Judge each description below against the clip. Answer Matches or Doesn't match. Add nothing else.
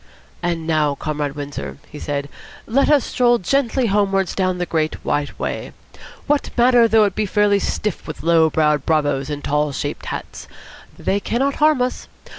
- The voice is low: Doesn't match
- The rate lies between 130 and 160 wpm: Doesn't match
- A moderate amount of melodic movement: Doesn't match